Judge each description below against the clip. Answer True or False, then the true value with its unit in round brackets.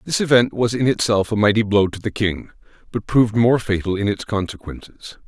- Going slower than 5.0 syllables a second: False (5.5 syllables/s)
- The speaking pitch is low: True (105 Hz)